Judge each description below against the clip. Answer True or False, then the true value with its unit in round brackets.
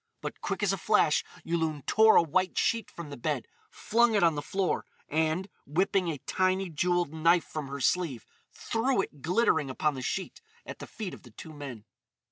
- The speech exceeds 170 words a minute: True (195 wpm)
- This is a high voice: False (165 Hz)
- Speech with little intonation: False (4.3 semitones)